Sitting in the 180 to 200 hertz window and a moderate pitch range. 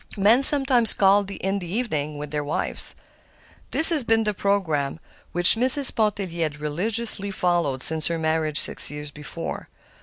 No: medium, 185 Hz; wide, 6.4 semitones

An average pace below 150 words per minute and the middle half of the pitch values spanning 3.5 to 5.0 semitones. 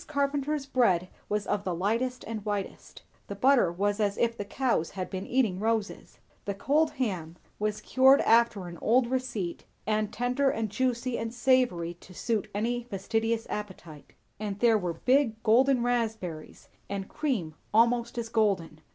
No: average, 160 wpm; average, 3.9 semitones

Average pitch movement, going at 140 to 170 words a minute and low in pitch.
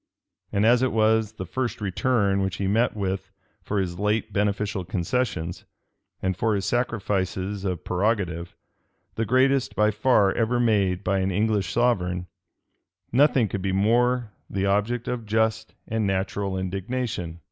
Yes: average, 3.1 semitones; average, 145 wpm; low, 105 Hz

